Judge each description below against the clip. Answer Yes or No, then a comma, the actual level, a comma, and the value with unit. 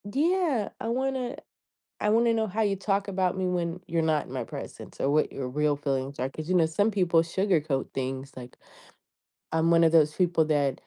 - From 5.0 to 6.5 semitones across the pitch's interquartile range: Yes, average, 5.3 semitones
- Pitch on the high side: No, medium, 170 Hz